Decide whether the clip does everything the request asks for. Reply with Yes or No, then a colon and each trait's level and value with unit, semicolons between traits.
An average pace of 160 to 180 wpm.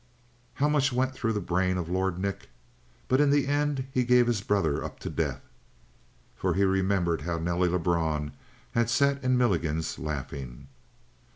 Yes: average, 165 wpm